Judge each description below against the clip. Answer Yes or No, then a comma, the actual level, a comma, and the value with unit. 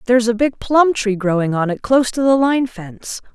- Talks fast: Yes, fast, 235 wpm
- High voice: Yes, high, 235 Hz